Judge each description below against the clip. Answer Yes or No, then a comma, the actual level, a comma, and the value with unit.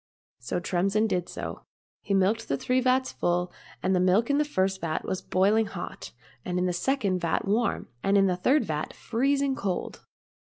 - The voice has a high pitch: Yes, high, 195 Hz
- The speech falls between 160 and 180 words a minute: No, average, 190 wpm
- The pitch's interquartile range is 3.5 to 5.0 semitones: Yes, average, 4.5 semitones